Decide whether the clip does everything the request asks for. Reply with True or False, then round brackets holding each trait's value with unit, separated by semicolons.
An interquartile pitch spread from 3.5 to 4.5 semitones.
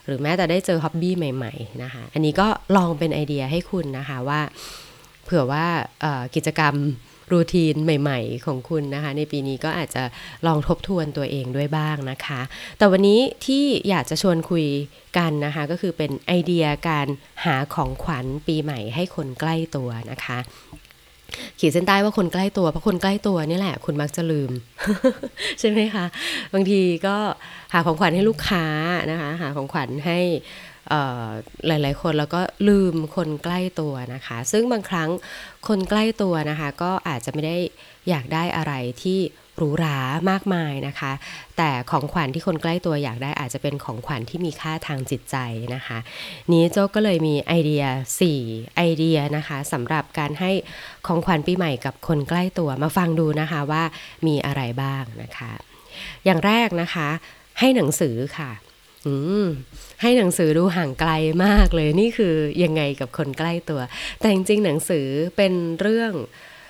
True (3.9 semitones)